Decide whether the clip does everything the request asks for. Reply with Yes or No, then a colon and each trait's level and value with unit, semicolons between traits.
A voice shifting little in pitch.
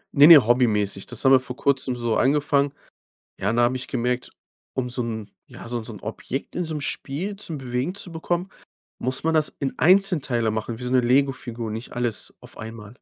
No: average, 3.5 semitones